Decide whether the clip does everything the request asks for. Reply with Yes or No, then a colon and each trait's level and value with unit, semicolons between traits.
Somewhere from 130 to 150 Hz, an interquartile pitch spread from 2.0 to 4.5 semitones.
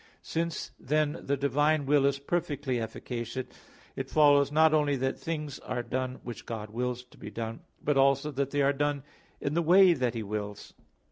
Yes: medium, 140 Hz; average, 3.0 semitones